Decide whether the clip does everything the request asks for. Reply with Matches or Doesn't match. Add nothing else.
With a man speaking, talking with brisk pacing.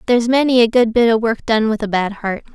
Doesn't match